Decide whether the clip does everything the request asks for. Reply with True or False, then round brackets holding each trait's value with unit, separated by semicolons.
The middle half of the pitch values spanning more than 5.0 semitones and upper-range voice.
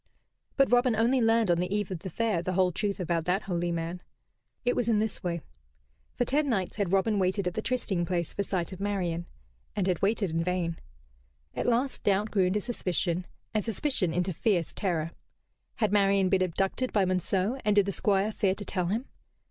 False (3.2 semitones; 195 Hz)